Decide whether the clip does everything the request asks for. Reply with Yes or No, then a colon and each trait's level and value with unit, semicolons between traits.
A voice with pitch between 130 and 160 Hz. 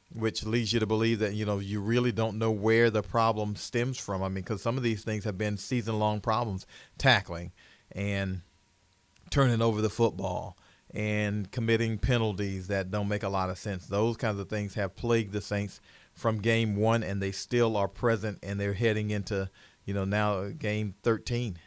No: low, 105 Hz